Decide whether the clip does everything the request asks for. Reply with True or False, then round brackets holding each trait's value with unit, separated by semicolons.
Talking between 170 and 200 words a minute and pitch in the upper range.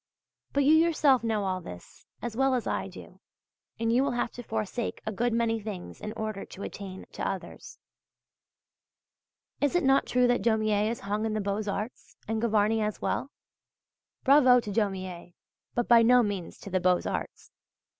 True (180 wpm; 220 Hz)